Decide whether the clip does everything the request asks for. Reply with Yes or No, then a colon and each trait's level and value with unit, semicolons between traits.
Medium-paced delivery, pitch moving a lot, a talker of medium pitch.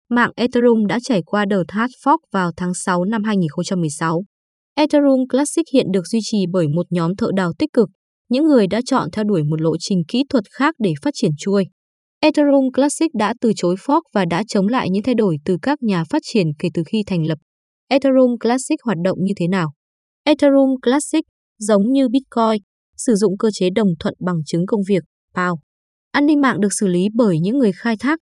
No: average, 210 wpm; wide, 6.1 semitones; high, 215 Hz